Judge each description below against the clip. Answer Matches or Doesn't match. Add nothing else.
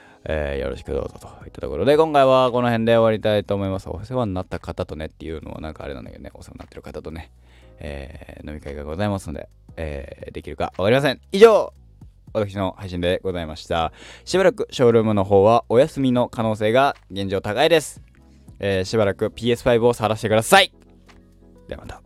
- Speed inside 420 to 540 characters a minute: Matches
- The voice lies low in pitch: Matches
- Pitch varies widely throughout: Matches